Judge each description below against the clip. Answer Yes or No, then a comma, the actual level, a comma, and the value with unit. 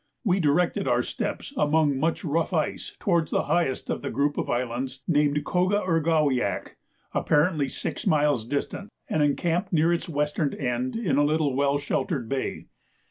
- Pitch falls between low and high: Yes, medium, 150 Hz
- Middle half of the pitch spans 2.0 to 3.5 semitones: Yes, average, 3.1 semitones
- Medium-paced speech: Yes, average, 170 wpm